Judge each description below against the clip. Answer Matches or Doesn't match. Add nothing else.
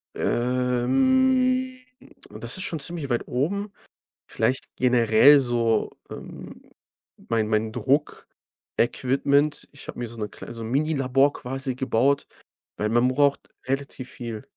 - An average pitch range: Matches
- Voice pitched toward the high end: Doesn't match